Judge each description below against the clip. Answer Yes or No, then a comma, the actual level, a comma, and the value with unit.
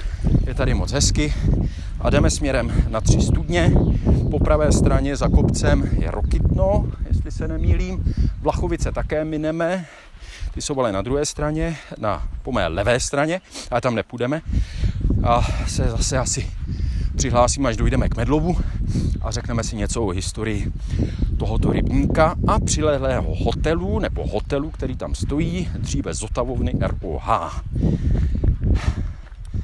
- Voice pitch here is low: Yes, very low, 95 Hz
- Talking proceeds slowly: No, average, 130 wpm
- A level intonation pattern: No, wide, 6.0 semitones